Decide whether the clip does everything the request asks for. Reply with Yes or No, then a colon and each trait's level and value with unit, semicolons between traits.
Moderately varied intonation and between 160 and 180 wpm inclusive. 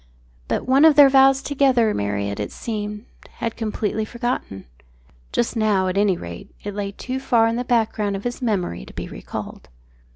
Yes: average, 3.9 semitones; average, 175 wpm